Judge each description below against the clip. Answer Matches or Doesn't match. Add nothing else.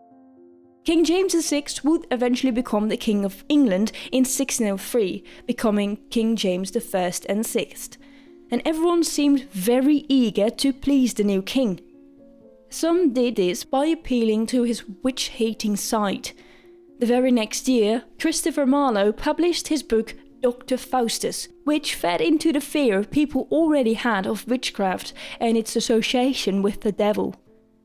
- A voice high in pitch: Matches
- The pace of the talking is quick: Doesn't match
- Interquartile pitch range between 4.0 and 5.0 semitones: Matches